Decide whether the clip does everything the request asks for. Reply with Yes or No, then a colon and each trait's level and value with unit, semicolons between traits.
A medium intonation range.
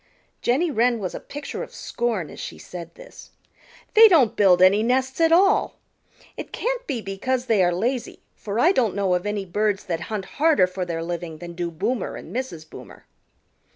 No: wide, 6.4 semitones